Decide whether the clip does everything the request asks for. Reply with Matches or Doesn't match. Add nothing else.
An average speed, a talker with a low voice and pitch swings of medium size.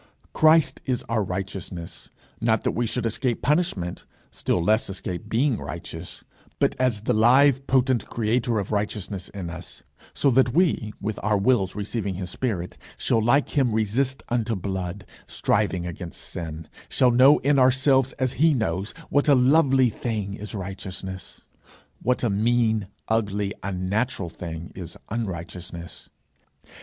Matches